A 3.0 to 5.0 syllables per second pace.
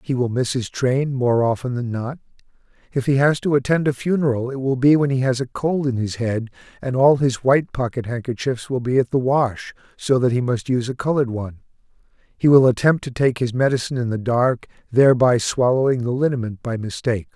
No: 5.7 syllables/s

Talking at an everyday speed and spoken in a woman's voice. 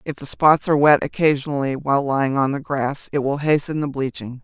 No: fast, 215 wpm; female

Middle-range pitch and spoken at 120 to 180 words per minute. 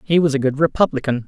No: medium, 145 Hz; fast, 235 wpm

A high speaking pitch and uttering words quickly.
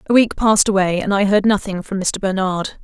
Yes: high, 200 Hz; fast, 235 wpm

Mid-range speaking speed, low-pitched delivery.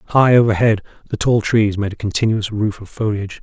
Yes: average, 195 wpm; low, 105 Hz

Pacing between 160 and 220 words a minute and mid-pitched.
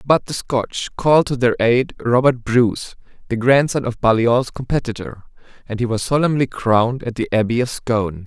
No: average, 175 wpm; low, 120 Hz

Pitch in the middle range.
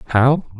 No: low, 130 Hz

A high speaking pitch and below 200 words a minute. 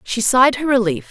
No: high, 230 Hz; fast, 215 wpm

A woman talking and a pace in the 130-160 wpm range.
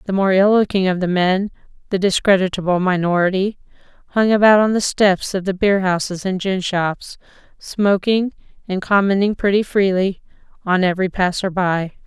Yes: female; average, 145 wpm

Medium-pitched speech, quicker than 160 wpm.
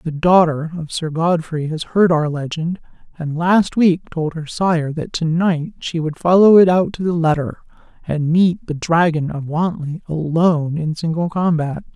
Yes: medium, 165 Hz; average, 180 wpm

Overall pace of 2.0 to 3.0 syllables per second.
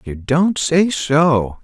Yes: 2.6 syllables/s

